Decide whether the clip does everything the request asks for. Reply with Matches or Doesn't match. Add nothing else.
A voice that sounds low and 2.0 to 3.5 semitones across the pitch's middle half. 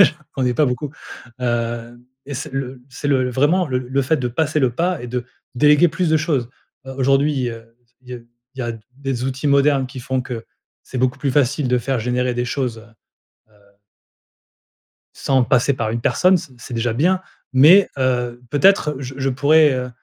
Matches